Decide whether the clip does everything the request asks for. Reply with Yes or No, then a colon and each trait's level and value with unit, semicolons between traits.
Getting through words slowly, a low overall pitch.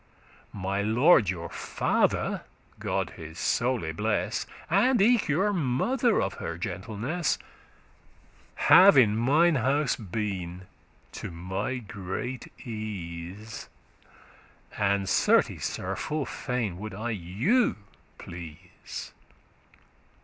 Yes: slow, 100 wpm; low, 110 Hz